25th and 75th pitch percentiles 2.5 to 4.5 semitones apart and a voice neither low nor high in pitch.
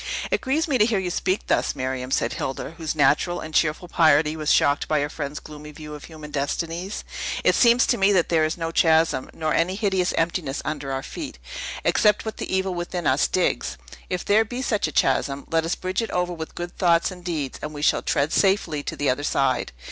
Yes: average, 3.9 semitones; medium, 165 Hz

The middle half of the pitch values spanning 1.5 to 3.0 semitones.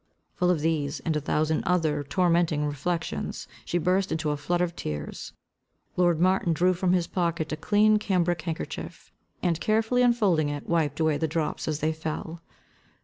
Yes: average, 2.7 semitones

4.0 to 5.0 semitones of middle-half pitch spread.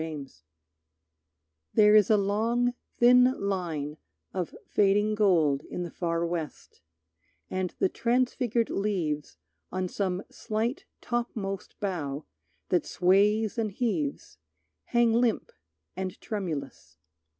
Yes: average, 4.7 semitones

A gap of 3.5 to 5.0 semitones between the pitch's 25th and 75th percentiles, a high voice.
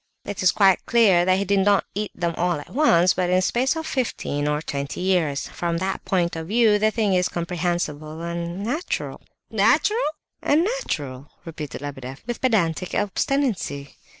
No: average, 4.7 semitones; medium, 180 Hz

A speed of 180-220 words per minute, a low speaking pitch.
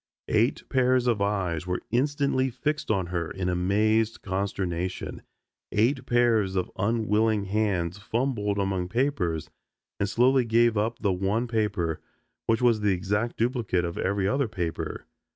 No: average, 140 wpm; low, 105 Hz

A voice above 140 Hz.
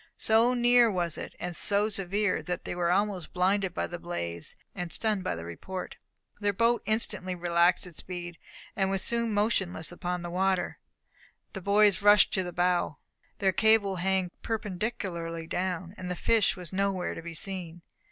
Yes: medium, 185 Hz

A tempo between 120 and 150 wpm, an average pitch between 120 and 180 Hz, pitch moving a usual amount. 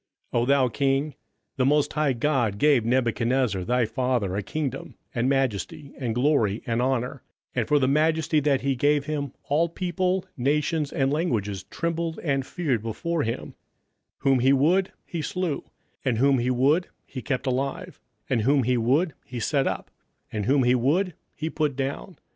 No: average, 175 wpm; low, 135 Hz; average, 3.6 semitones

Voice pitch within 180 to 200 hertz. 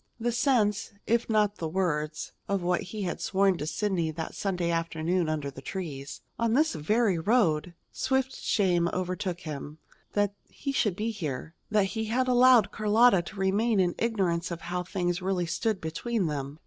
Yes: high, 190 Hz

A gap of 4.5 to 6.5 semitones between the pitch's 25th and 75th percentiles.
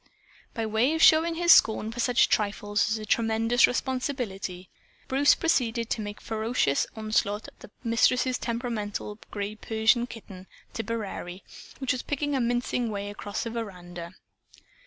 No: average, 3.1 semitones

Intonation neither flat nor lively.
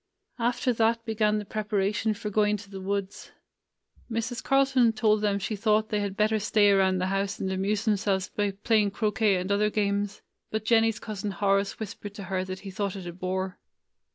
No: narrow, 1.8 semitones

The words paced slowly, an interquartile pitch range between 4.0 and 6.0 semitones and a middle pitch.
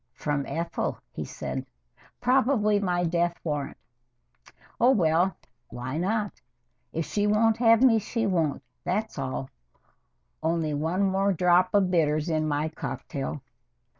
Yes: slow, 130 wpm; average, 5.1 semitones; medium, 175 Hz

